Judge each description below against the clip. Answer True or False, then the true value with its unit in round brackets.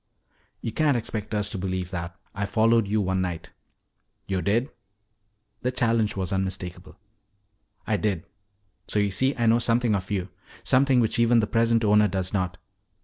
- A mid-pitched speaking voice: False (105 Hz)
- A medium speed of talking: True (165 wpm)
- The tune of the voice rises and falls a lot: False (3.6 semitones)